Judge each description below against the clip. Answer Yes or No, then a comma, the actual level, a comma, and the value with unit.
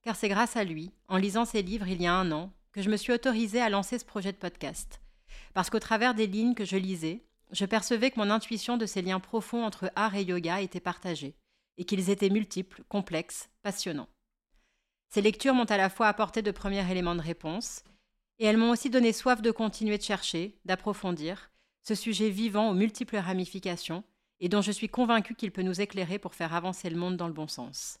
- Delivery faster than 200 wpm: Yes, average, 215 wpm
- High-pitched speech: Yes, high, 205 Hz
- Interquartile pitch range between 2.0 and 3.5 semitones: Yes, average, 3.2 semitones